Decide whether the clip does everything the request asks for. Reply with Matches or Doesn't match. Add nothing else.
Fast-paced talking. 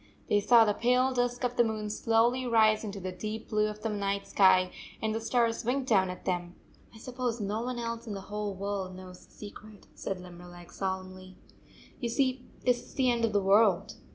Matches